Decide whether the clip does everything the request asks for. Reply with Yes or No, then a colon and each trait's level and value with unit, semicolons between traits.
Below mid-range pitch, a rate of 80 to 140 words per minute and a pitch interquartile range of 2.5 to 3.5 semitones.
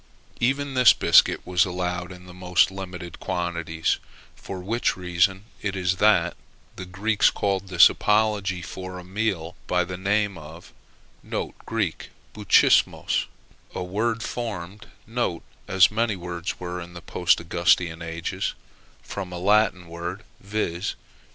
Yes: very low, 90 Hz; slow, 135 wpm; average, 2.8 semitones